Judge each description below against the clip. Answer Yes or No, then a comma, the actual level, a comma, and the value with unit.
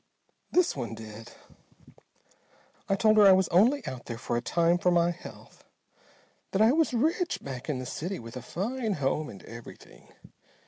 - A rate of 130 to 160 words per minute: No, average, 175 wpm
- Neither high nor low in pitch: Yes, medium, 170 Hz